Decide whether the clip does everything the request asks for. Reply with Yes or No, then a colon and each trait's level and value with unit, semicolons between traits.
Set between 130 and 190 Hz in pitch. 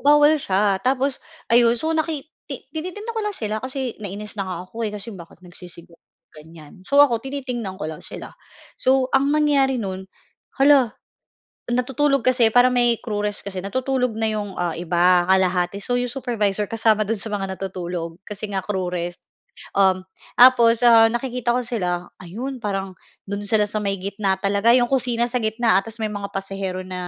No: high, 220 Hz